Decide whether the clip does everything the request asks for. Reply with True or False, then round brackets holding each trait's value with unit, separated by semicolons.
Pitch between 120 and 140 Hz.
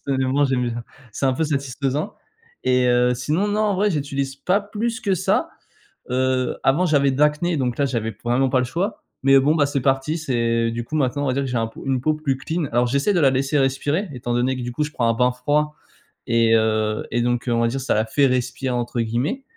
True (135 Hz)